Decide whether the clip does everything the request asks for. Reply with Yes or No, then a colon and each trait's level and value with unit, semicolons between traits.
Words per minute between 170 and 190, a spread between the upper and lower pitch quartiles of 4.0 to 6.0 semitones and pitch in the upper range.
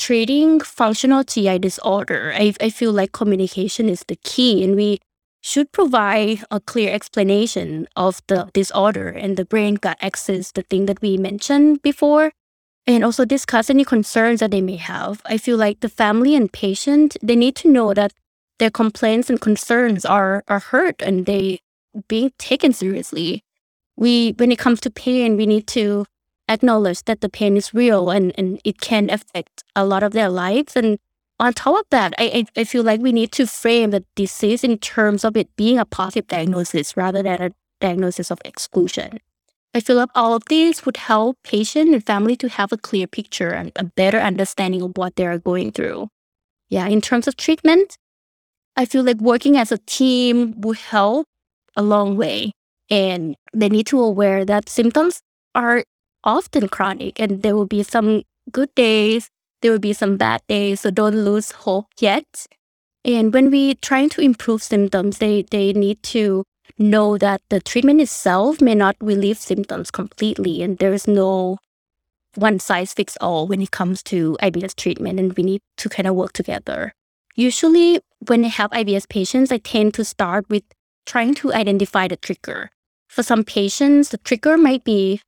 No: average, 180 wpm; average, 3.5 semitones; high, 215 Hz